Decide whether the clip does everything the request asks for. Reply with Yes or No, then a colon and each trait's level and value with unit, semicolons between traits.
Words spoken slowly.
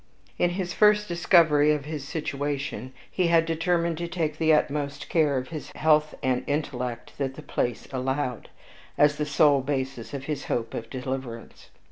No: average, 165 wpm